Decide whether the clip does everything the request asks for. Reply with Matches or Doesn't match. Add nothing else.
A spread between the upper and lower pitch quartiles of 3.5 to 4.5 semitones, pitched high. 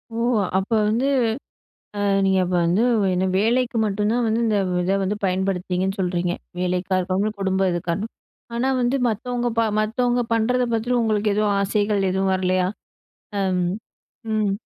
Doesn't match